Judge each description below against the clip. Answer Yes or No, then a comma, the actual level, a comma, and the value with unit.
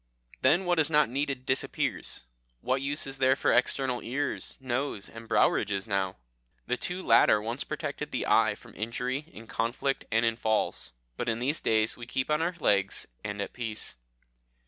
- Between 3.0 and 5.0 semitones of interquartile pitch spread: Yes, average, 3.7 semitones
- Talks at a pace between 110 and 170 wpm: No, average, 180 wpm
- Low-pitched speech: Yes, low, 125 Hz